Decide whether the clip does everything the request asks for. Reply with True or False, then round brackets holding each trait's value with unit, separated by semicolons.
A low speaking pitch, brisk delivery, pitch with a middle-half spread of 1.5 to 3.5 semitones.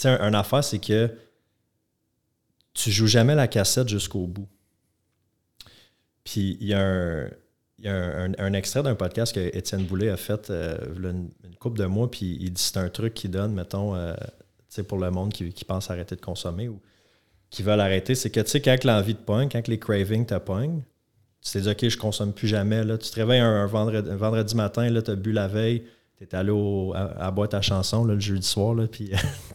True (105 Hz; 230 wpm; 2.8 semitones)